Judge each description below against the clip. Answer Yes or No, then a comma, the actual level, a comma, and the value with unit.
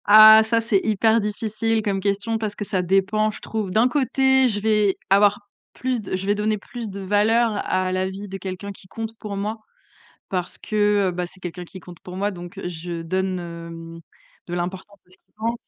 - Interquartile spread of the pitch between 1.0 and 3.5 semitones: Yes, average, 2.7 semitones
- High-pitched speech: Yes, high, 200 Hz